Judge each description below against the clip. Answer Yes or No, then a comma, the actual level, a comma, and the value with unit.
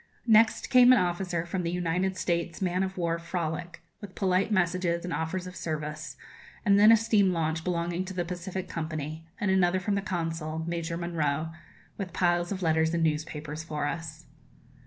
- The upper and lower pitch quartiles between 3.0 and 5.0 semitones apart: No, narrow, 2.5 semitones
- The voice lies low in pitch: No, medium, 175 Hz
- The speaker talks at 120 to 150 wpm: No, average, 180 wpm